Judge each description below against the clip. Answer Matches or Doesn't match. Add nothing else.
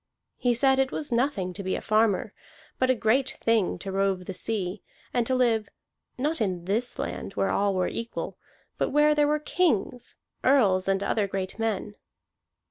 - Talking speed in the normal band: Matches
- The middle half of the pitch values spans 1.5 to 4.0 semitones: Doesn't match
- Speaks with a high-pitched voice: Matches